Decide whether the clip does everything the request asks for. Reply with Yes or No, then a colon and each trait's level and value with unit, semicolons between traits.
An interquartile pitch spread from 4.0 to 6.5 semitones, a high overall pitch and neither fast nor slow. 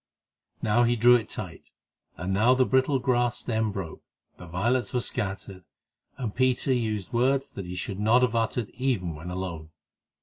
No: average, 4.7 semitones; low, 110 Hz; average, 170 wpm